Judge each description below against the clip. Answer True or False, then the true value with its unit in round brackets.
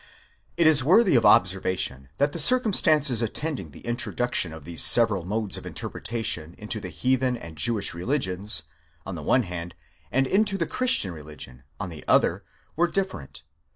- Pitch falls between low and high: False (115 Hz)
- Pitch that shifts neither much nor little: False (8.7 semitones)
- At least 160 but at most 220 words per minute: True (165 wpm)